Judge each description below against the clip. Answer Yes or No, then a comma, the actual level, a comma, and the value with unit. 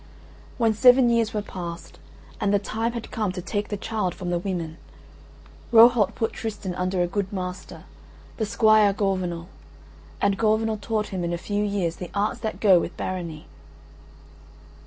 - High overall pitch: Yes, high, 200 Hz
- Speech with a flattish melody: No, average, 3.2 semitones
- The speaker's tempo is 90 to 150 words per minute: No, average, 165 wpm